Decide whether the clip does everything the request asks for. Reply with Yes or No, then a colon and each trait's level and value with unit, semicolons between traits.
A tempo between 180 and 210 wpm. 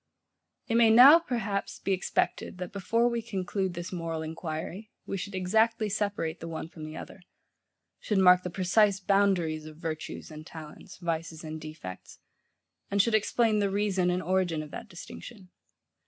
No: average, 165 wpm